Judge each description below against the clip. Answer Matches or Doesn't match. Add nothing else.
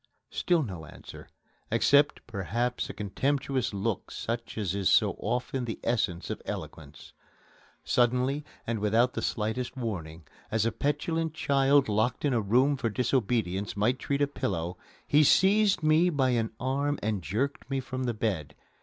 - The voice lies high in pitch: Doesn't match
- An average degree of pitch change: Matches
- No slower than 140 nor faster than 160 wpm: Matches